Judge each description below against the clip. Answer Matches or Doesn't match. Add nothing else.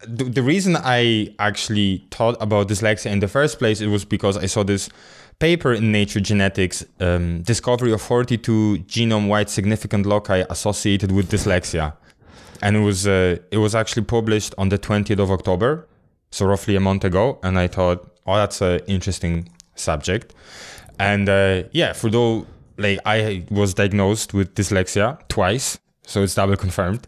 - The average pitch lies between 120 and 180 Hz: Doesn't match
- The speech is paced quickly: Doesn't match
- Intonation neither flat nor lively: Doesn't match